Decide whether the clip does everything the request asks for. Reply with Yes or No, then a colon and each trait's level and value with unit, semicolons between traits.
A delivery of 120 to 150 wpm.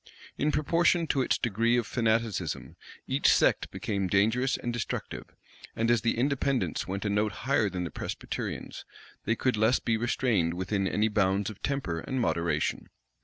No: average, 165 wpm